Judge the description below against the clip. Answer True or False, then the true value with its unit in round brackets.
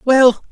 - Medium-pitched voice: False (245 Hz)